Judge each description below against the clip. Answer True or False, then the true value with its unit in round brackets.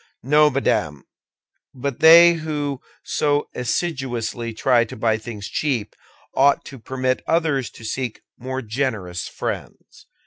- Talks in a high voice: False (130 Hz)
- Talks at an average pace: False (125 wpm)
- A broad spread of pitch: False (4.1 semitones)